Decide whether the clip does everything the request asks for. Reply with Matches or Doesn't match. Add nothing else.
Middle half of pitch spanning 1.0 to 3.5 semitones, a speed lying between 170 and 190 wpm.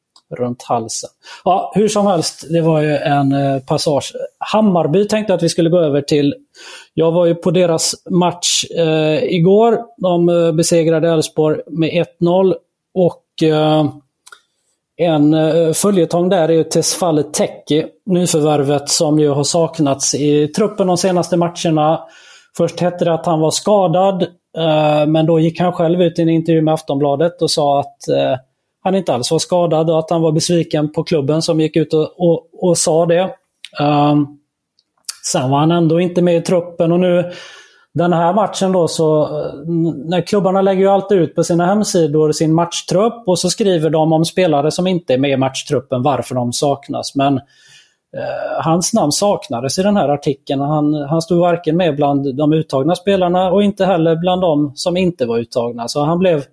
Matches